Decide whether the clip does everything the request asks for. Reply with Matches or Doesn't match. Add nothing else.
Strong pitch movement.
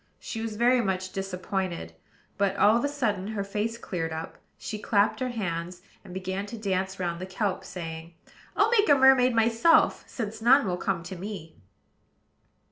Doesn't match